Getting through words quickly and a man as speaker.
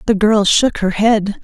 No: fast, 210 wpm; female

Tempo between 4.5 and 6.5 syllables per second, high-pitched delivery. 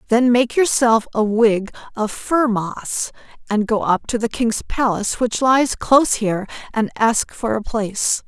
No: 4.3 syllables/s; high, 225 Hz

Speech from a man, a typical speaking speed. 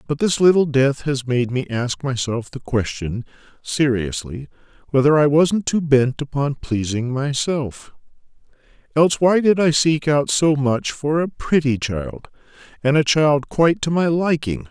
Yes: male; average, 160 wpm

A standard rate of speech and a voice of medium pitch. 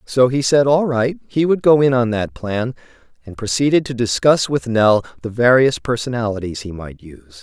No: average, 195 wpm; low, 120 Hz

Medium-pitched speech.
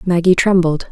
Yes: medium, 175 Hz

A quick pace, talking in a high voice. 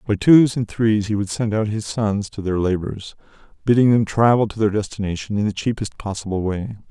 No: fast, 210 wpm; low, 105 Hz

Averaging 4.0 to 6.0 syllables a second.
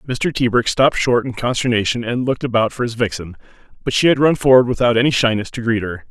No: 6.4 syllables/s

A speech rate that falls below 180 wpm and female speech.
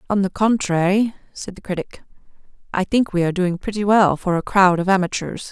No: average, 195 wpm; female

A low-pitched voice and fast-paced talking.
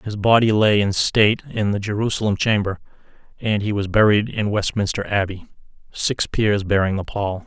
No: low, 105 Hz; average, 170 wpm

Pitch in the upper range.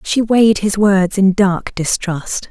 Yes: high, 195 Hz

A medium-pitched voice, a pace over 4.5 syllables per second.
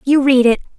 No: very high, 265 Hz; 6.0 syllables/s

